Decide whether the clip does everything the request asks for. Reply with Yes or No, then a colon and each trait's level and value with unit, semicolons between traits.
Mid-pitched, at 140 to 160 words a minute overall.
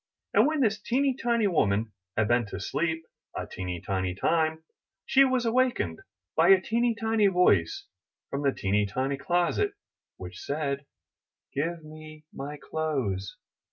Yes: medium, 155 Hz; average, 145 wpm